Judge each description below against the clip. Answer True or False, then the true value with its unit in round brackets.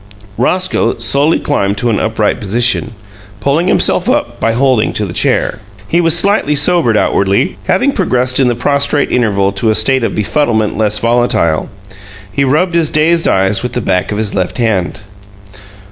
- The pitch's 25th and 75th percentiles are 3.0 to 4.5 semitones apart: False (5.5 semitones)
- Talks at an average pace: True (170 wpm)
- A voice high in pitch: False (120 Hz)